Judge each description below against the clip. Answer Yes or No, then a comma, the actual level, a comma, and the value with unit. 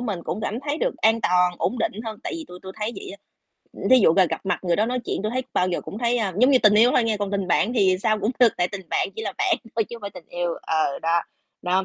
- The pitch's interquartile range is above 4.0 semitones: Yes, average, 4.5 semitones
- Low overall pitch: No, high, 210 Hz